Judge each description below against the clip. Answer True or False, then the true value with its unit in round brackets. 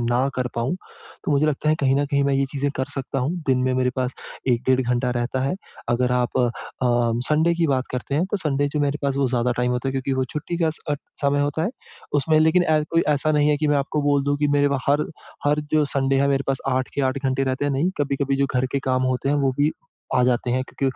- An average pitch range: False (2.1 semitones)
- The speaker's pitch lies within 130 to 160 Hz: True (140 Hz)